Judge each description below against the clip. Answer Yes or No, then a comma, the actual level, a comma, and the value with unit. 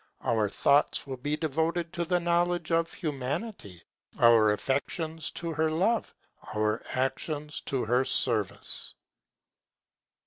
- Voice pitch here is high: No, medium, 150 Hz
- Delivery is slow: Yes, slow, 115 wpm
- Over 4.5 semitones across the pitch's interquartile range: Yes, average, 5.1 semitones